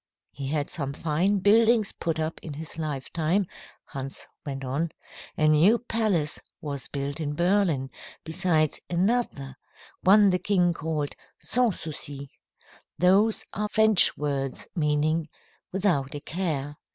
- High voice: No, medium, 160 Hz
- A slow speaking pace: Yes, slow, 125 wpm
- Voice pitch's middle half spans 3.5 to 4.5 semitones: No, average, 5.0 semitones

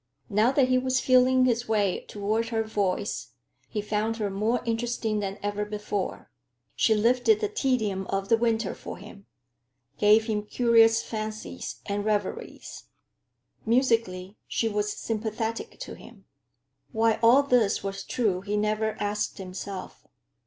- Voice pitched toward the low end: No, high, 220 Hz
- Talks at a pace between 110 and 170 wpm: Yes, average, 140 wpm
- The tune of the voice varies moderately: No, narrow, 2.2 semitones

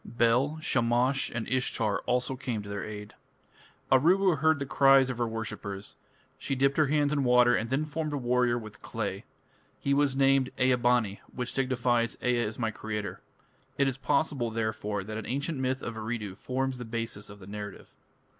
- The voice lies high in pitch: No, low, 125 Hz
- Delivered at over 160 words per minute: Yes, average, 185 wpm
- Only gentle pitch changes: No, average, 3.4 semitones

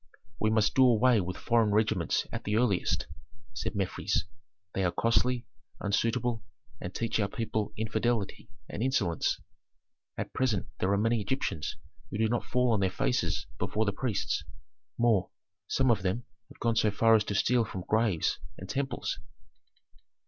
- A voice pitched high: No, low, 110 Hz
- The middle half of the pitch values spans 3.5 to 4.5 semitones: No, average, 3.0 semitones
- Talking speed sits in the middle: Yes, average, 160 wpm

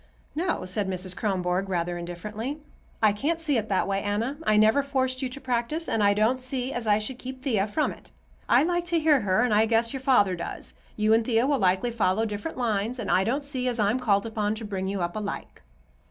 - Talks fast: Yes, fast, 230 wpm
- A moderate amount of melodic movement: Yes, average, 4.3 semitones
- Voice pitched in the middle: No, high, 225 Hz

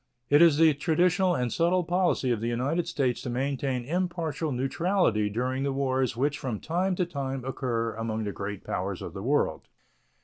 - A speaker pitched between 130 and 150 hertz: Yes, low, 135 Hz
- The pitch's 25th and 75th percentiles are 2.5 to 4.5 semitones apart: No, wide, 5.6 semitones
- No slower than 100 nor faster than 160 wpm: No, average, 180 wpm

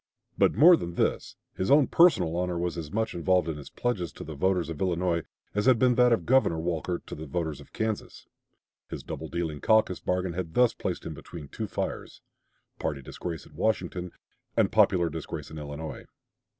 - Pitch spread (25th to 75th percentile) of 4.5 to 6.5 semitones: Yes, average, 5.1 semitones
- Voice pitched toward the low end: Yes, very low, 90 Hz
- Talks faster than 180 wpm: Yes, average, 190 wpm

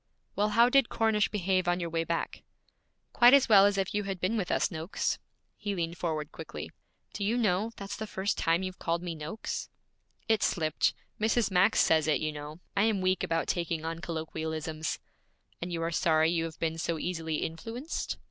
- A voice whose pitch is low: No, medium, 175 Hz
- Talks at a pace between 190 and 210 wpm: Yes, average, 195 wpm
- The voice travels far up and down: No, average, 3.9 semitones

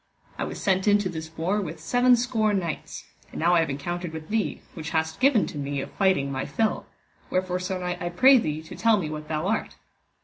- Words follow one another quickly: Yes, fast, 225 wpm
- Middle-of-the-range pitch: Yes, medium, 180 Hz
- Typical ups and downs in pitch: Yes, average, 4.6 semitones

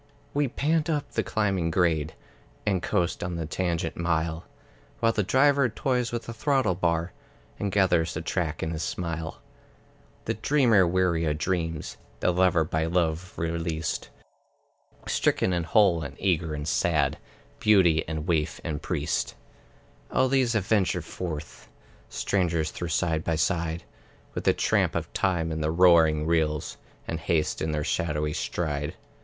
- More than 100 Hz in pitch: No, very low, 85 Hz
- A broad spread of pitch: No, average, 3.2 semitones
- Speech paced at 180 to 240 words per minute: No, average, 150 wpm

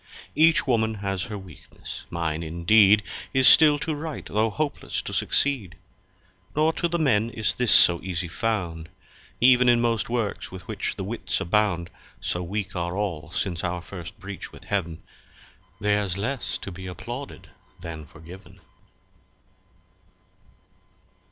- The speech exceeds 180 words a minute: No, average, 140 wpm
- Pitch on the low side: Yes, low, 100 Hz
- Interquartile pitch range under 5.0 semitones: No, average, 5.3 semitones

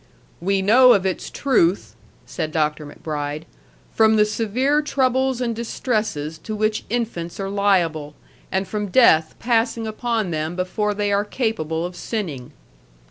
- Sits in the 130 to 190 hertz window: No, high, 205 Hz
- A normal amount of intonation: No, wide, 5.8 semitones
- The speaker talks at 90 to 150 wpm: Yes, average, 140 wpm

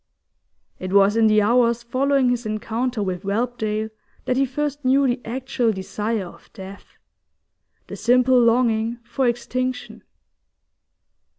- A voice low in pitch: No, high, 235 Hz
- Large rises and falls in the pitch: No, average, 2.9 semitones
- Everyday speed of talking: No, slow, 125 wpm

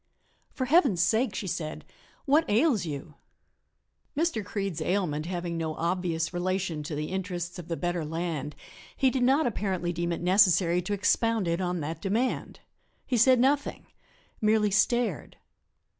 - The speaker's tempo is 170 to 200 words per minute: No, average, 150 wpm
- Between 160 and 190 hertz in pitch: Yes, medium, 185 Hz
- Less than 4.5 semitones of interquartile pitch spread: No, average, 4.9 semitones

